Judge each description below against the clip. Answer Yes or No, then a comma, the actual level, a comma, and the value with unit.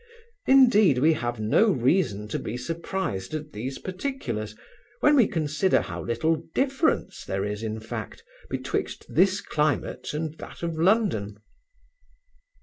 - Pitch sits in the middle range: Yes, medium, 155 Hz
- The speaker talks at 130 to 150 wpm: Yes, slow, 135 wpm